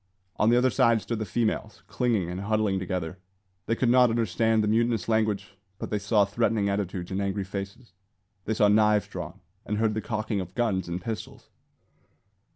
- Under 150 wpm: No, average, 180 wpm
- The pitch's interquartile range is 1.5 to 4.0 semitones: Yes, narrow, 2.5 semitones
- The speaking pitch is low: Yes, low, 105 Hz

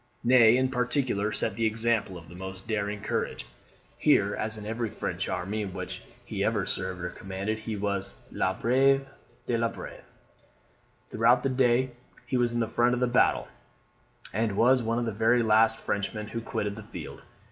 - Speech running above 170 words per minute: Yes, average, 180 wpm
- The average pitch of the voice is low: Yes, low, 110 Hz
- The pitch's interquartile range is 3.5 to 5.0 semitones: No, average, 3.0 semitones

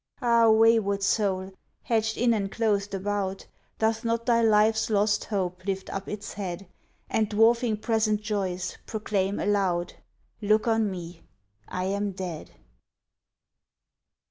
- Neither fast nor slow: No, slow, 125 wpm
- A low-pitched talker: No, high, 205 Hz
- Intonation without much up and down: Yes, narrow, 2.3 semitones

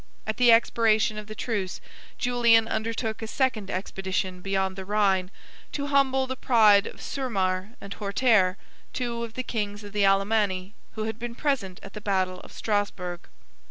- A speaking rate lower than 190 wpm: Yes, average, 165 wpm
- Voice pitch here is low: No, high, 215 Hz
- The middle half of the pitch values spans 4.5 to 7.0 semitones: No, average, 3.2 semitones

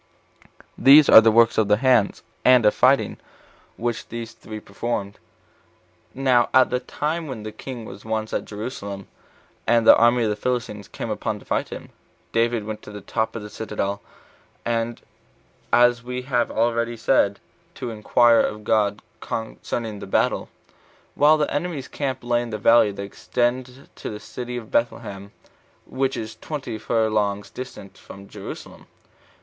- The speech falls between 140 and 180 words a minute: Yes, average, 160 wpm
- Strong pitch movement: No, average, 2.9 semitones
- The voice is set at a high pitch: No, low, 115 Hz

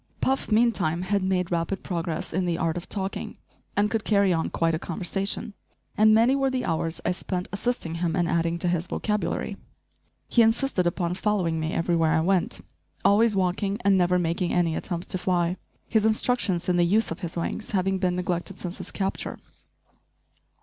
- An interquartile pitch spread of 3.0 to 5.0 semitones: Yes, average, 3.3 semitones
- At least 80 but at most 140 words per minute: No, average, 185 wpm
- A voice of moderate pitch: Yes, medium, 180 Hz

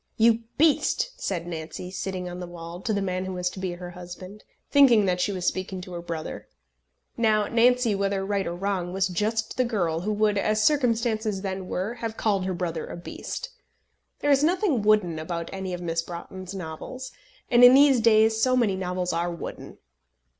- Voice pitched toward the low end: No, high, 195 Hz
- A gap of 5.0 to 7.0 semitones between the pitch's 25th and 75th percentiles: No, average, 4.0 semitones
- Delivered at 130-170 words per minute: No, average, 195 wpm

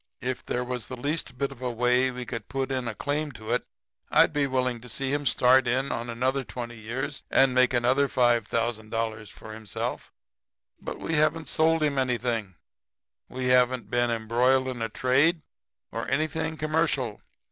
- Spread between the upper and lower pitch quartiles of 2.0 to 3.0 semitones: Yes, narrow, 2.5 semitones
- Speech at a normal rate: Yes, average, 175 wpm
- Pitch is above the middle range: No, low, 125 Hz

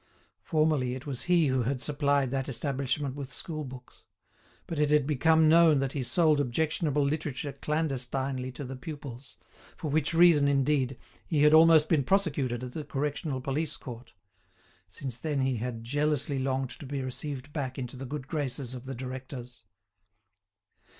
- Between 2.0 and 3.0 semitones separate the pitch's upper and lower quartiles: Yes, average, 2.7 semitones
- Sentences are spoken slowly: No, average, 165 wpm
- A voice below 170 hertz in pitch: Yes, medium, 140 Hz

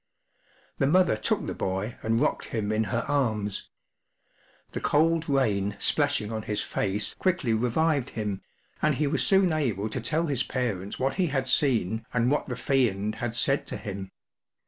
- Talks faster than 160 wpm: Yes, average, 170 wpm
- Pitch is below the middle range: Yes, low, 120 Hz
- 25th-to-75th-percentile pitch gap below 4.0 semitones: No, average, 5.3 semitones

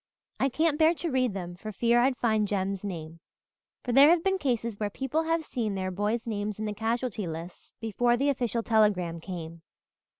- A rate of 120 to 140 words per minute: No, average, 195 wpm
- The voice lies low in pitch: No, high, 220 Hz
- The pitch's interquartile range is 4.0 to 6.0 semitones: Yes, average, 4.9 semitones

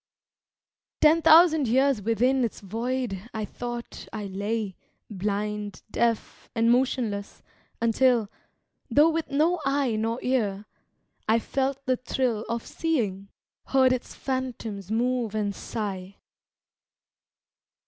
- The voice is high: Yes, high, 235 Hz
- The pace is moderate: No, slow, 110 wpm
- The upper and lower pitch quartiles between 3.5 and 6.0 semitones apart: Yes, average, 3.8 semitones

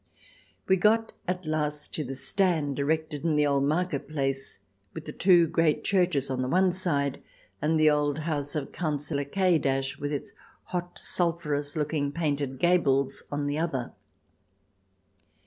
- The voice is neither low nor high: Yes, medium, 150 Hz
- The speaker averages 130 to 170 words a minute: Yes, average, 165 wpm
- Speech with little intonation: No, average, 3.2 semitones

